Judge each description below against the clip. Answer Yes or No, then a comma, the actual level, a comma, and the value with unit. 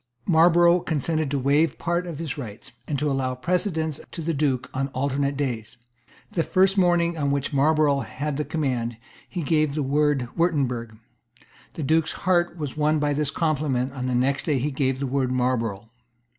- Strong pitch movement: No, average, 3.4 semitones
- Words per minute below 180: No, average, 185 wpm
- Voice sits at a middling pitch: Yes, medium, 145 Hz